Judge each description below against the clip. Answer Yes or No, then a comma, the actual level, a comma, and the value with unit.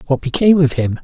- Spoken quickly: Yes, fast, 235 wpm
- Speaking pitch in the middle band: Yes, medium, 145 Hz